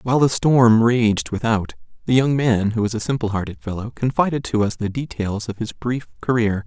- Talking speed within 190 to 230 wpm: Yes, fast, 205 wpm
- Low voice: Yes, low, 115 Hz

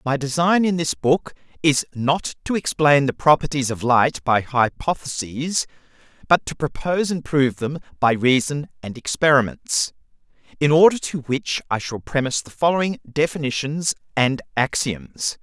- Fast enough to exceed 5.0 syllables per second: No, 4.7 syllables/s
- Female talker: No, male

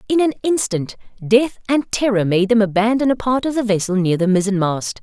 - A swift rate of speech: Yes, fast, 215 wpm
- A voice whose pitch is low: No, high, 215 Hz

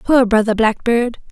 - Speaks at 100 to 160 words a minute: Yes, slow, 135 wpm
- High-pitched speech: Yes, high, 230 Hz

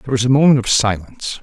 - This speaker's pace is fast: Yes, fast, 250 wpm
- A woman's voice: No, male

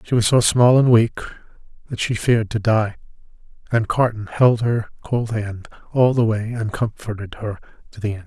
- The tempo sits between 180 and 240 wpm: Yes, average, 190 wpm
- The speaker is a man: Yes, male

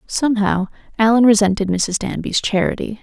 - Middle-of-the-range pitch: No, high, 210 Hz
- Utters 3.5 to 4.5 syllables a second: No, 5.4 syllables/s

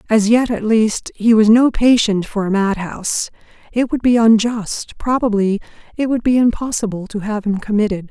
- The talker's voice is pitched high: Yes, high, 220 Hz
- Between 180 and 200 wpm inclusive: Yes, average, 185 wpm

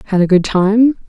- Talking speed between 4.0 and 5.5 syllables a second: Yes, 5.2 syllables/s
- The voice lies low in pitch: No, high, 205 Hz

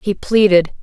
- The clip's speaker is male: No, female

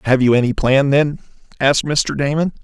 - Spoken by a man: Yes, male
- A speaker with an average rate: Yes, average, 185 wpm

